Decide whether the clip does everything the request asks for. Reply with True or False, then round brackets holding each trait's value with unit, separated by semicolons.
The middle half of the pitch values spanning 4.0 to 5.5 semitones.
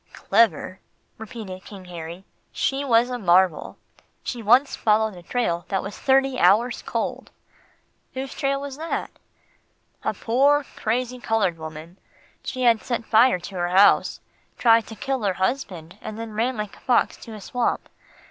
True (5.0 semitones)